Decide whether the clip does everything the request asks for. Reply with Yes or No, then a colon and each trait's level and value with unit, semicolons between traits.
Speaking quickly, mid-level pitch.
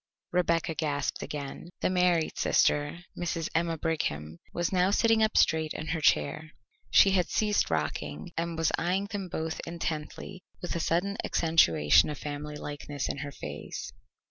No: average, 155 wpm; medium, 160 Hz